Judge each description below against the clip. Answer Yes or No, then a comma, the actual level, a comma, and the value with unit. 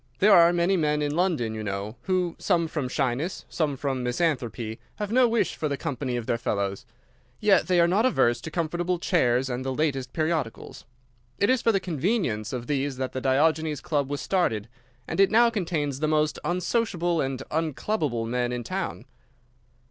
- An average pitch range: No, wide, 5.7 semitones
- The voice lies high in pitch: No, medium, 150 Hz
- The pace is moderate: Yes, average, 185 wpm